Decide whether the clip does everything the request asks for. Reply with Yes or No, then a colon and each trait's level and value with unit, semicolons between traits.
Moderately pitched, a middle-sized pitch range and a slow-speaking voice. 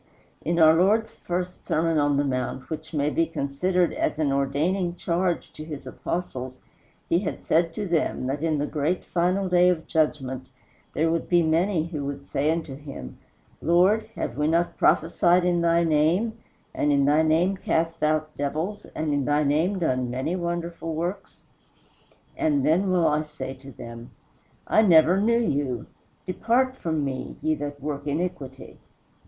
No: medium, 160 Hz; average, 3.7 semitones; average, 170 wpm